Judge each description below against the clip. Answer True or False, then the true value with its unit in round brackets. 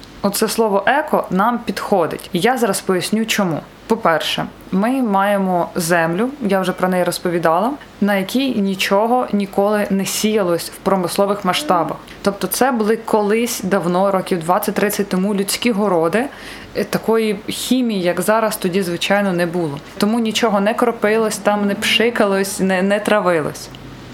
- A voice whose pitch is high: True (200 Hz)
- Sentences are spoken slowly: False (140 wpm)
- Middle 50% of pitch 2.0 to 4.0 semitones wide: True (2.9 semitones)